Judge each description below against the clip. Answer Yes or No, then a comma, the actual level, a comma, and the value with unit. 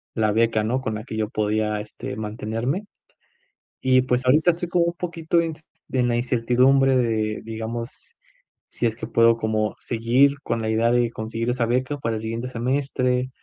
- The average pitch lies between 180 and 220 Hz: No, low, 120 Hz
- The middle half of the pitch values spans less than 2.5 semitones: No, average, 2.8 semitones